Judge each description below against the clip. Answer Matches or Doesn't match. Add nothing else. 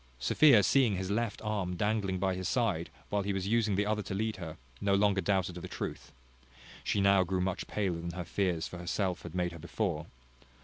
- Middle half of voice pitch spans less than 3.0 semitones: Matches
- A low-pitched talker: Matches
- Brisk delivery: Matches